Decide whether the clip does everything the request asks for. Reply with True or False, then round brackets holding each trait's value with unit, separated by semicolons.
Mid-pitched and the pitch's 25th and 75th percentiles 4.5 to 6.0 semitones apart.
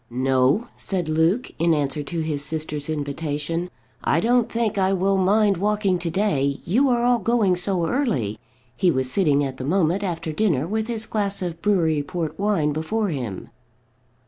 True (175 Hz; 5.6 semitones)